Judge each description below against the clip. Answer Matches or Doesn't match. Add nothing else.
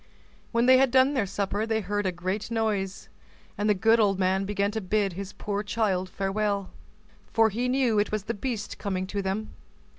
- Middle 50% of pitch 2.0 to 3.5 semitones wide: Matches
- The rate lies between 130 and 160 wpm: Doesn't match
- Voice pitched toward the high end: Matches